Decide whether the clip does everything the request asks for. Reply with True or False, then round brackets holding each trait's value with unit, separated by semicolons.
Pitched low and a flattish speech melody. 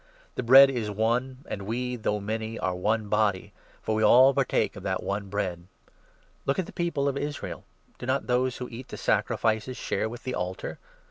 False (115 Hz; 3.7 semitones)